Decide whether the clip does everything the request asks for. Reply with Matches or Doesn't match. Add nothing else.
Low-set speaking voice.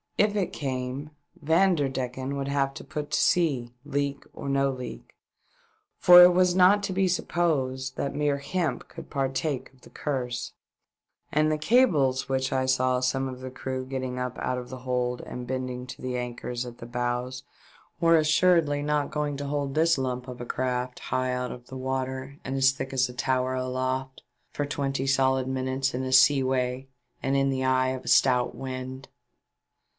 Matches